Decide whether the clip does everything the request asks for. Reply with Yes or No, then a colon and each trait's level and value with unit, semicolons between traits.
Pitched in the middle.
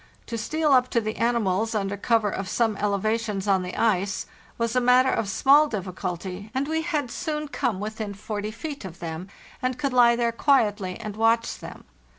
No: high, 225 Hz